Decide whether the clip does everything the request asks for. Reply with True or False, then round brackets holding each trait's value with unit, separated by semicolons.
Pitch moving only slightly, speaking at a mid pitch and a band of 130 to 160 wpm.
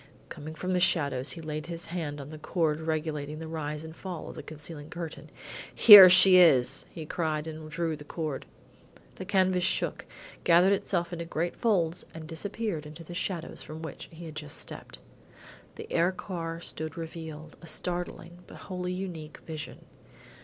False (2.3 semitones; 165 Hz; 175 wpm)